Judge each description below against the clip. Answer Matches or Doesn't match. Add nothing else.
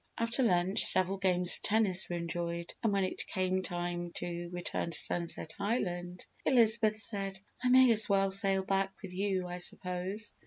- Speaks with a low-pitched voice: Doesn't match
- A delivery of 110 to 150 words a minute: Doesn't match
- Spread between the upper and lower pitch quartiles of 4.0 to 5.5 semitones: Doesn't match